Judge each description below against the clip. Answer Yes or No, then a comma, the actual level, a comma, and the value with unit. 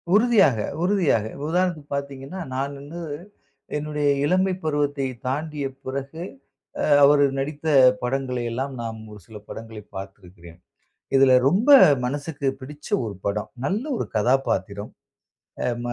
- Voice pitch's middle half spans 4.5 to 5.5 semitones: No, average, 3.8 semitones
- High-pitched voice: No, medium, 140 Hz